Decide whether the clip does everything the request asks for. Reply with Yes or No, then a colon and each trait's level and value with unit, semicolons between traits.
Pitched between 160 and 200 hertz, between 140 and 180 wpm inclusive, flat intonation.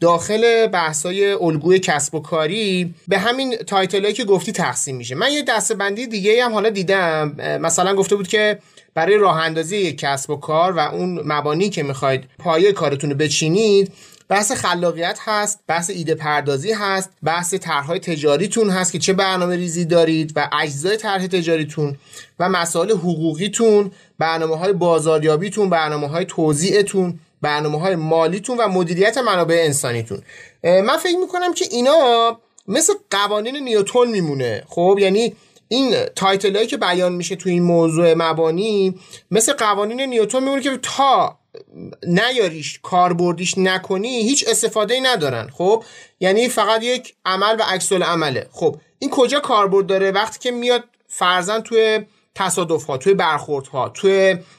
No: high, 190 Hz; average, 150 wpm; average, 4.8 semitones